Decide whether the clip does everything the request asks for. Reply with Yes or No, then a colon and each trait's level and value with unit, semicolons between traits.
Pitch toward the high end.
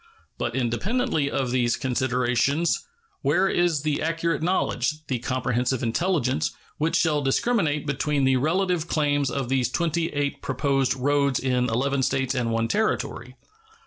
No: medium, 140 Hz